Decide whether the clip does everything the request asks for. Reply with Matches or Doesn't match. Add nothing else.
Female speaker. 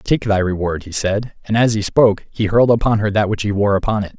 Doesn't match